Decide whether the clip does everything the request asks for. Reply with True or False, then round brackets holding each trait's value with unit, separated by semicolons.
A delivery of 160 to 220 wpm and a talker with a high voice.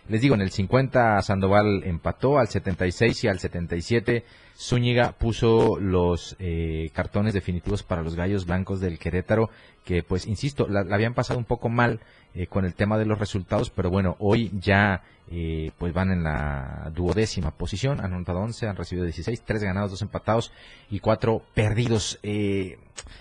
False (170 wpm; 100 Hz)